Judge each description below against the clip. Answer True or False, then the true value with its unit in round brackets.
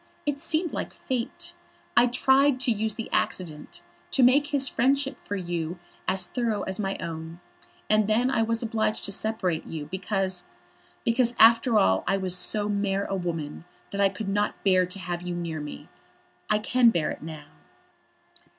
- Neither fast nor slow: True (175 wpm)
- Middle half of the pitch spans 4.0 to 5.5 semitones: True (4.9 semitones)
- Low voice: False (205 Hz)